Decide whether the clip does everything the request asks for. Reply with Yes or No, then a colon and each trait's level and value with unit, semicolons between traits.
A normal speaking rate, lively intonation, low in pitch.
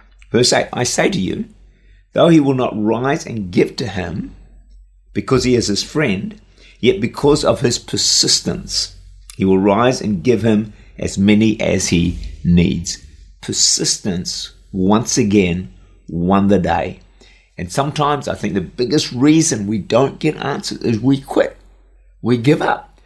Yes: average, 155 wpm; wide, 6.3 semitones; low, 105 Hz